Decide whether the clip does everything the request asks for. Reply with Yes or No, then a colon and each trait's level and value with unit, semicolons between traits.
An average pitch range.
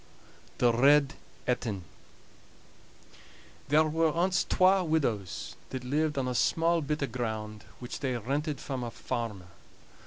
Yes: average, 4.7 semitones